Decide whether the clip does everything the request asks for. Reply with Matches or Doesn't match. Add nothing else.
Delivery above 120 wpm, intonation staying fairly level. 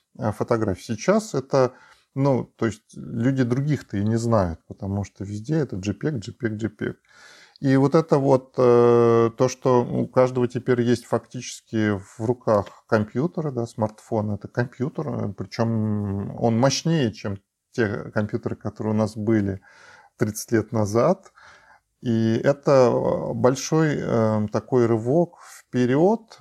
Doesn't match